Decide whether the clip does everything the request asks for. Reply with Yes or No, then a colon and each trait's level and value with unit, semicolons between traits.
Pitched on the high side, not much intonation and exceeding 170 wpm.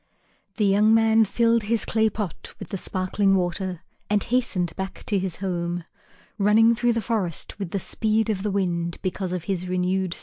No: high, 195 Hz; average, 3.2 semitones; average, 190 wpm